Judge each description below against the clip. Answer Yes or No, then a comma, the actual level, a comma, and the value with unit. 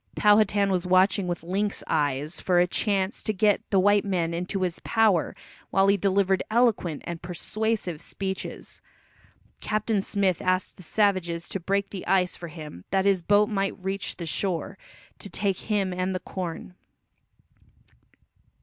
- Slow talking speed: No, average, 155 wpm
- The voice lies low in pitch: No, high, 190 Hz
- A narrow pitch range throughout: Yes, narrow, 2.3 semitones